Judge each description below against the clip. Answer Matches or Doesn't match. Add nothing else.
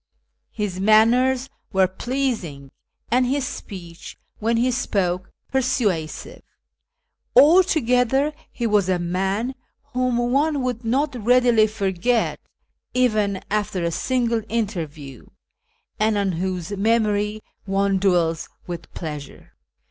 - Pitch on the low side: Doesn't match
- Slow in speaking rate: Matches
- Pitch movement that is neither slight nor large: Matches